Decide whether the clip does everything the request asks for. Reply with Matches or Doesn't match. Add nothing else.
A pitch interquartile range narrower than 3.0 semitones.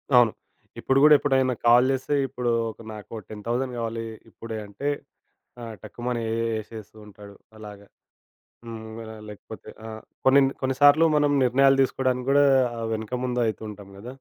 Doesn't match